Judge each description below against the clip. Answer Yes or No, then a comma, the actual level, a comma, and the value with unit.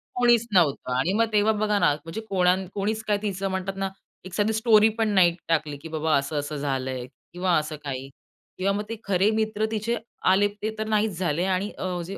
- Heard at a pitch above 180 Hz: Yes, high, 190 Hz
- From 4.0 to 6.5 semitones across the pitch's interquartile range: Yes, average, 4.8 semitones